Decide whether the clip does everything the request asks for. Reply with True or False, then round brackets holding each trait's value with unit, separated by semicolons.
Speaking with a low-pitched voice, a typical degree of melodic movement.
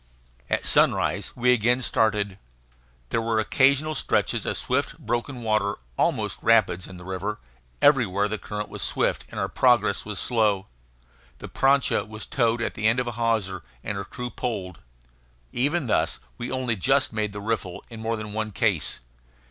True (110 Hz; 3.0 semitones)